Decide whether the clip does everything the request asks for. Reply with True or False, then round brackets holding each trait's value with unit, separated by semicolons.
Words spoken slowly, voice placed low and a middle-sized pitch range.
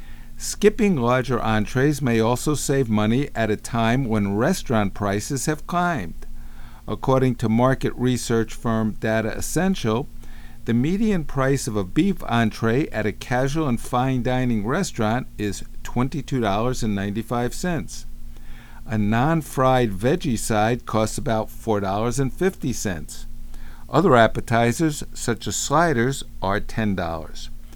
True (115 wpm; 120 Hz; 3.1 semitones)